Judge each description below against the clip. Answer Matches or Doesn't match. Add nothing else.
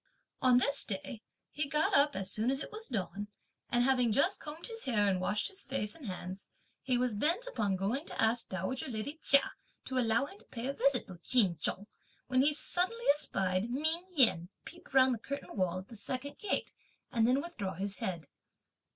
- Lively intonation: Matches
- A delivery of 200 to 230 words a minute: Matches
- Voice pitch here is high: Matches